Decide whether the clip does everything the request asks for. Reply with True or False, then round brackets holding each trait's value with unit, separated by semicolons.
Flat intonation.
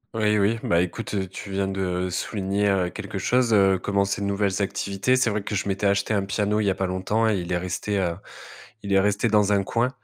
True (1.6 semitones)